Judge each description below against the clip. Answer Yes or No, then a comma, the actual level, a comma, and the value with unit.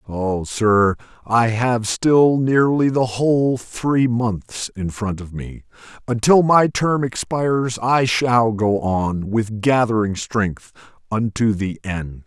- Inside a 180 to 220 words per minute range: No, slow, 135 wpm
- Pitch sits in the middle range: No, low, 115 Hz